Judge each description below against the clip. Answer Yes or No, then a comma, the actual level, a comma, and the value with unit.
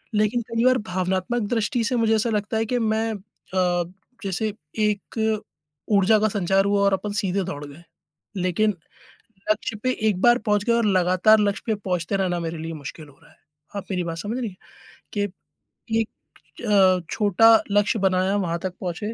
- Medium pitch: No, high, 200 Hz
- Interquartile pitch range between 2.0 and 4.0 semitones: Yes, average, 3.0 semitones